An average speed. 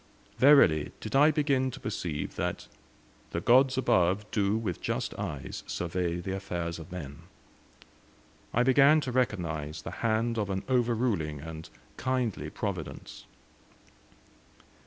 No: slow, 125 wpm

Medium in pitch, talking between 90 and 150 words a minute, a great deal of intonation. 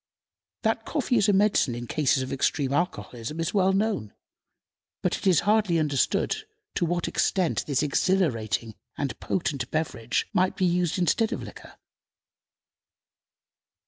Yes: medium, 165 Hz; average, 145 wpm; wide, 6.0 semitones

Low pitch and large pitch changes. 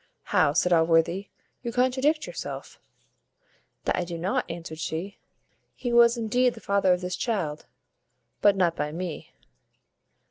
No: medium, 185 Hz; wide, 5.9 semitones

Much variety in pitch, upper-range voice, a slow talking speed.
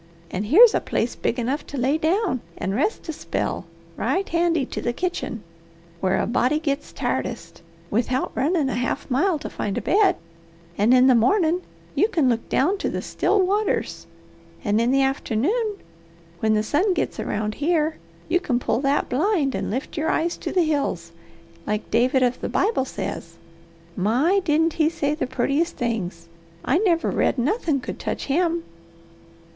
No: wide, 6.1 semitones; very high, 285 Hz; average, 175 wpm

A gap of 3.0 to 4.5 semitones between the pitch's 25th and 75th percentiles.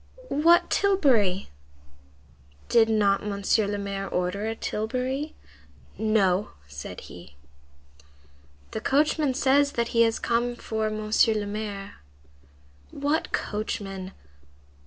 Yes: average, 4.1 semitones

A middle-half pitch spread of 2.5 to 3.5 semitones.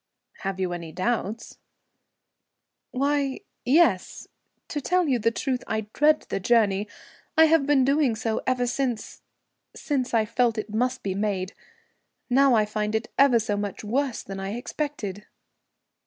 No: average, 4.7 semitones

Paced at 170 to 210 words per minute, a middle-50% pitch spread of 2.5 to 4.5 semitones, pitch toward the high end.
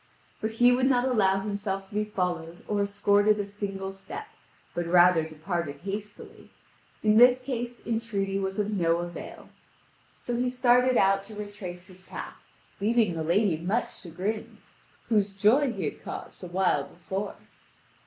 No: average, 155 wpm; average, 3.4 semitones; high, 200 Hz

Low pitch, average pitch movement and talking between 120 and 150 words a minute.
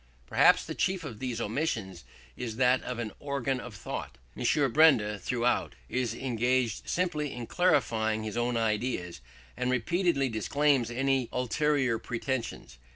Yes: low, 125 Hz; average, 3.4 semitones; average, 140 wpm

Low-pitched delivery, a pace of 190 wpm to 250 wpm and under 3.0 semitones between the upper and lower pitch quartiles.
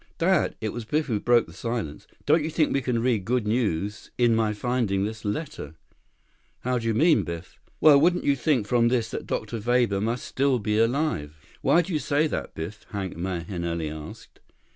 No: low, 115 Hz; average, 195 wpm; average, 5.1 semitones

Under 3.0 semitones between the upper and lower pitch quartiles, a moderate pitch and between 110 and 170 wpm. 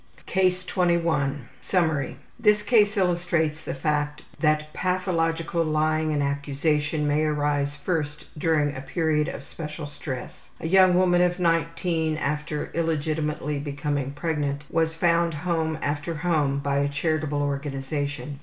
Yes: narrow, 2.4 semitones; medium, 155 Hz; slow, 135 wpm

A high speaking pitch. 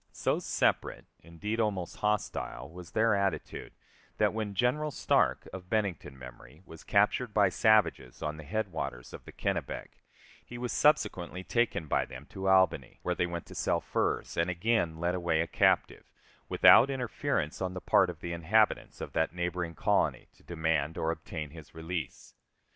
No: very low, 90 Hz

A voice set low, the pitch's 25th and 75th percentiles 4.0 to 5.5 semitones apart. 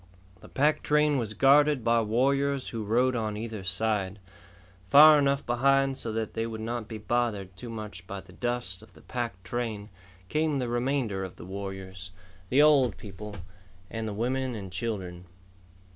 Yes: low, 115 Hz; average, 4.6 semitones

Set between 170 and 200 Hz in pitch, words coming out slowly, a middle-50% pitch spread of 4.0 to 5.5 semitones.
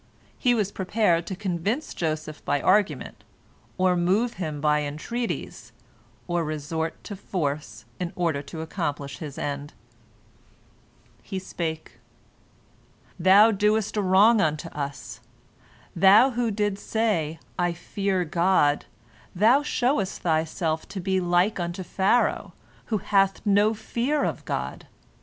Yes: medium, 185 Hz; slow, 125 wpm; average, 4.6 semitones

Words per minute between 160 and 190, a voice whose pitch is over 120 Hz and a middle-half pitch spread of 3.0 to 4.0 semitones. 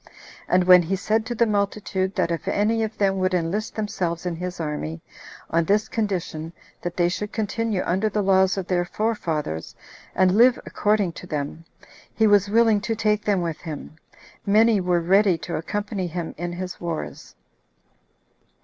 Yes: average, 170 wpm; high, 190 Hz; average, 3.4 semitones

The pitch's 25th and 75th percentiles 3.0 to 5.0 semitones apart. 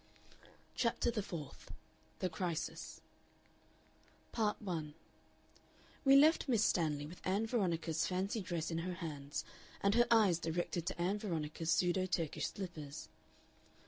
Yes: average, 4.3 semitones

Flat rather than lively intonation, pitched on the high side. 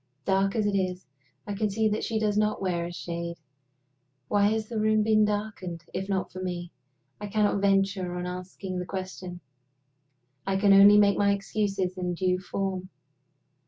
Yes: narrow, 2.1 semitones; high, 195 Hz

